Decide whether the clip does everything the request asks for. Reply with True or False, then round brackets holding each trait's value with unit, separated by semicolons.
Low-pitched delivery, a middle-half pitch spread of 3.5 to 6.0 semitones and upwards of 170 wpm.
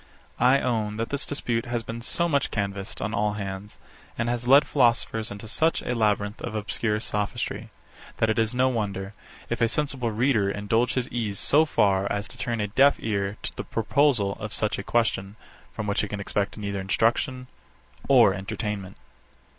False (110 Hz; 3.0 semitones; 185 wpm)